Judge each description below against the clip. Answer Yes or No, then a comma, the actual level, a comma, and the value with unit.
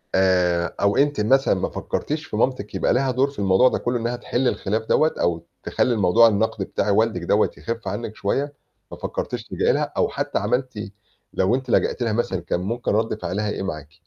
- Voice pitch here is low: Yes, low, 110 Hz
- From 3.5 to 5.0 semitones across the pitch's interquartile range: Yes, average, 4.3 semitones